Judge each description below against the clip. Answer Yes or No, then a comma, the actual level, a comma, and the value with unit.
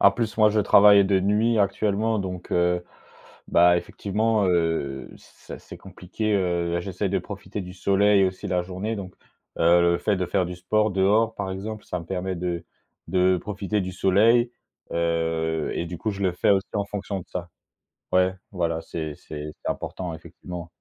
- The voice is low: Yes, very low, 95 Hz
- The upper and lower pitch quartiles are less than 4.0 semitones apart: Yes, average, 2.8 semitones